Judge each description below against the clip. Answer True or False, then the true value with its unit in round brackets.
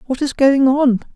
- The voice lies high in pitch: True (270 Hz)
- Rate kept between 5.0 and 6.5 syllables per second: False (4.7 syllables/s)